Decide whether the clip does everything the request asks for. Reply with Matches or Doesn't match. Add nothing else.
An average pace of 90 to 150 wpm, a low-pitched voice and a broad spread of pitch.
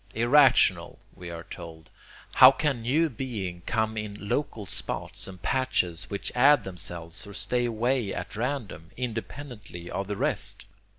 Matches